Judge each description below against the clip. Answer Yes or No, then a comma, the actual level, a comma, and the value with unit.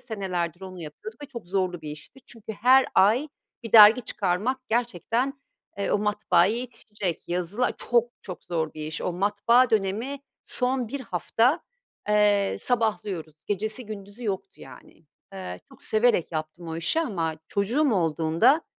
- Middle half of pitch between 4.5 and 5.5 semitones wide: Yes, average, 5.2 semitones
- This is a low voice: No, high, 210 Hz